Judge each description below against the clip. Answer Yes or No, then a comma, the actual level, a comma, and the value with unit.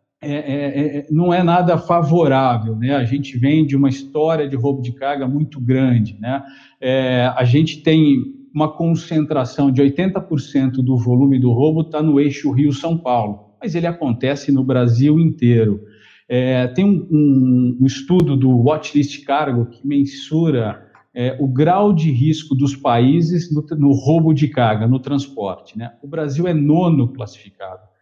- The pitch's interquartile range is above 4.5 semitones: No, average, 3.2 semitones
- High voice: No, medium, 140 Hz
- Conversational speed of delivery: Yes, average, 160 wpm